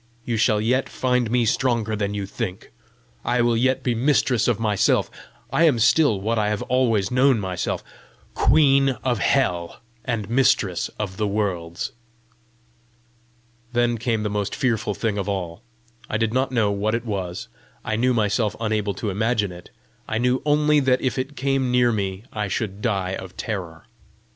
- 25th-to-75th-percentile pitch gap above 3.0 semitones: Yes, average, 3.7 semitones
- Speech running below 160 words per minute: No, average, 170 wpm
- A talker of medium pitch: No, low, 110 Hz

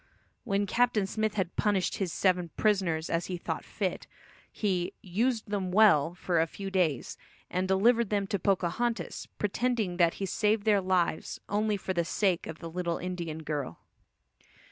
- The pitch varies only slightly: No, average, 3.3 semitones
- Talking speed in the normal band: Yes, average, 165 wpm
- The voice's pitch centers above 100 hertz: Yes, high, 190 Hz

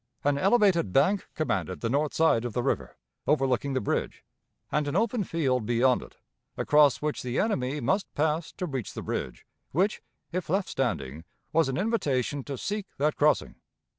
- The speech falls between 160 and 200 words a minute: Yes, average, 170 wpm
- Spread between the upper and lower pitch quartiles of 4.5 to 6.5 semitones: Yes, average, 5.1 semitones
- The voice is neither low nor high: Yes, medium, 145 Hz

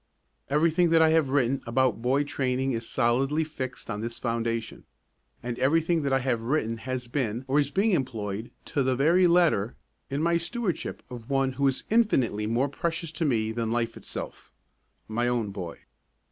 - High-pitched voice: No, low, 130 Hz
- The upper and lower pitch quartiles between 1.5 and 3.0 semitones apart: No, average, 4.9 semitones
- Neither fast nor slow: Yes, average, 175 wpm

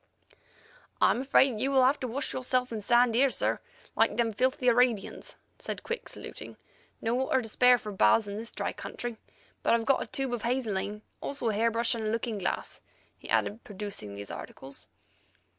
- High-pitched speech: Yes, high, 235 Hz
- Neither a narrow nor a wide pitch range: Yes, average, 3.1 semitones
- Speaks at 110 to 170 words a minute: No, average, 190 wpm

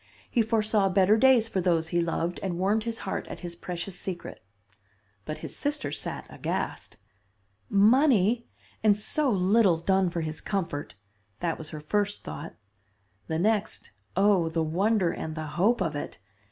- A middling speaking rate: Yes, average, 160 wpm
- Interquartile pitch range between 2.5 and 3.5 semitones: No, average, 4.4 semitones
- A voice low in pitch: No, high, 190 Hz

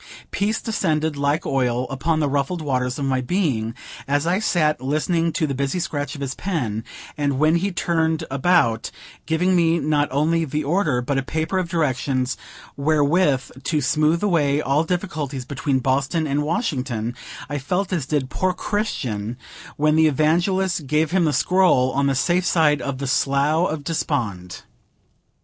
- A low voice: No, medium, 150 Hz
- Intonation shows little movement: No, average, 3.7 semitones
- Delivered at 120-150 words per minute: No, average, 165 wpm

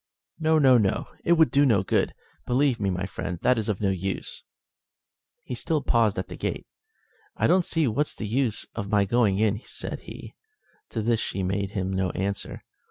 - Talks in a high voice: No, low, 110 Hz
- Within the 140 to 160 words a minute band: No, average, 200 wpm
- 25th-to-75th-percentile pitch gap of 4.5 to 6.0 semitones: Yes, average, 4.9 semitones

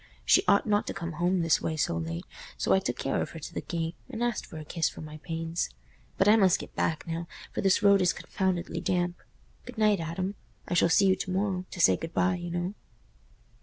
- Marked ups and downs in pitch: No, average, 2.8 semitones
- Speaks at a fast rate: Yes, fast, 235 wpm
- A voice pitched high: No, medium, 175 Hz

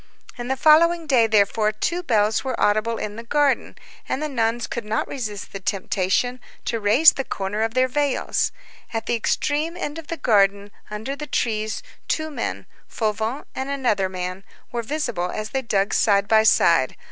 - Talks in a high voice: Yes, high, 225 Hz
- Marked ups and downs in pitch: No, average, 4.7 semitones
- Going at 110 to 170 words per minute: No, average, 180 wpm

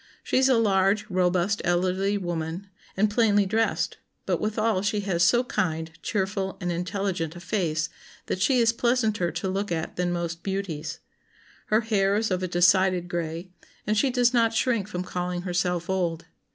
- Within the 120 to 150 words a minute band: No, average, 170 wpm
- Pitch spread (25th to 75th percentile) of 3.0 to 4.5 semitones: Yes, average, 3.3 semitones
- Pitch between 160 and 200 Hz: Yes, high, 190 Hz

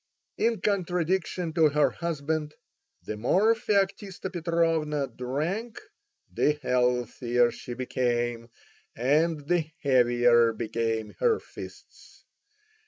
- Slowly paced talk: Yes, slow, 95 wpm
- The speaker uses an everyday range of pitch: No, wide, 6.3 semitones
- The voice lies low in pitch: No, medium, 150 Hz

